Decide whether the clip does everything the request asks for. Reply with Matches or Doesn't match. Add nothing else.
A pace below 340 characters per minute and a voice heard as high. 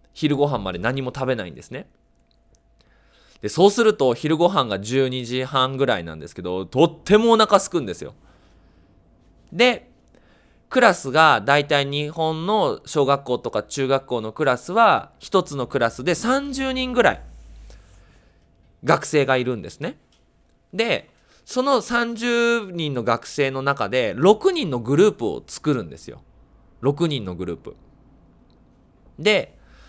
Doesn't match